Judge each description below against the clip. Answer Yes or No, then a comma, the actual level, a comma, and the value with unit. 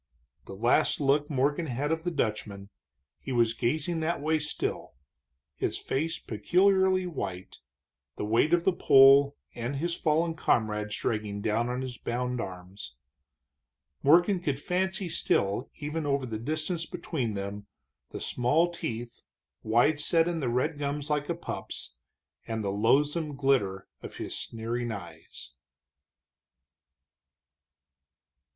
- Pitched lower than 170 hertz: Yes, low, 135 Hz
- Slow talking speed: Yes, slow, 130 wpm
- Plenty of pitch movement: Yes, wide, 6.1 semitones